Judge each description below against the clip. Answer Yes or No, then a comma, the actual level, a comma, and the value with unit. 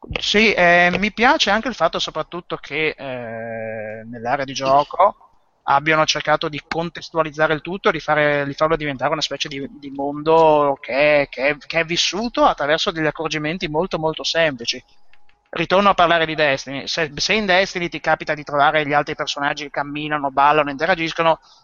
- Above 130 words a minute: Yes, fast, 170 wpm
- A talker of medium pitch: Yes, medium, 155 Hz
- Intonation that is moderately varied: Yes, average, 3.0 semitones